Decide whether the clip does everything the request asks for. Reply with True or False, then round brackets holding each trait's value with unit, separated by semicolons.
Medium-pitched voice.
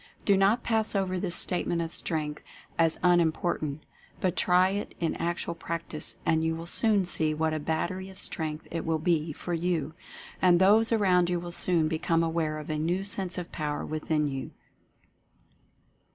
True (170 Hz)